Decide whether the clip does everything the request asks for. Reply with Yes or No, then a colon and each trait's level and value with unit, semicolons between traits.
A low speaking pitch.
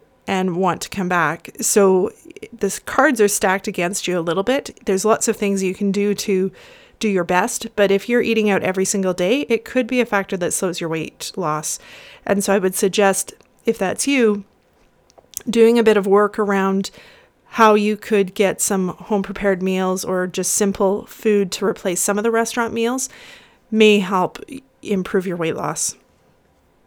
No: high, 200 Hz